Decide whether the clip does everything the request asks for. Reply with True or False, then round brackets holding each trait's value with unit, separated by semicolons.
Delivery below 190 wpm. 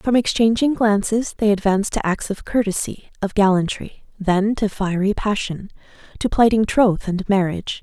True (155 wpm)